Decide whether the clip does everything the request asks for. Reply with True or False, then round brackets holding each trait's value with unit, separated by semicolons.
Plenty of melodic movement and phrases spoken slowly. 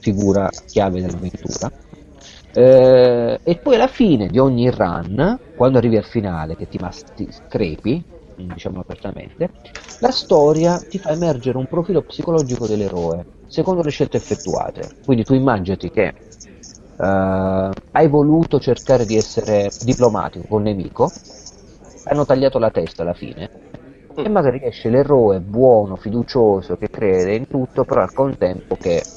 False (6.5 semitones; 140 wpm)